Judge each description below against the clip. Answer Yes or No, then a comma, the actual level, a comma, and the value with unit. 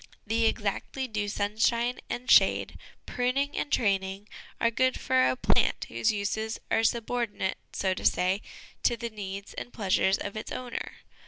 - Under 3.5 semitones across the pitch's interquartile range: Yes, average, 3.1 semitones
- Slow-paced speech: No, average, 160 wpm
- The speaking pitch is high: Yes, high, 220 Hz